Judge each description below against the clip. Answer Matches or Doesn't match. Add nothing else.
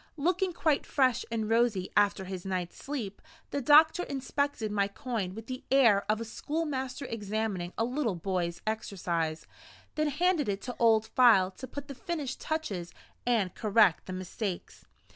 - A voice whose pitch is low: Doesn't match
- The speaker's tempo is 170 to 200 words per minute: Doesn't match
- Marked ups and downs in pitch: Matches